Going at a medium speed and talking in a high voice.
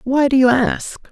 No: fast, 215 wpm; very high, 255 Hz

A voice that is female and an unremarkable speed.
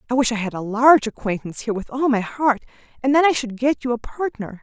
No: female; fast, 260 wpm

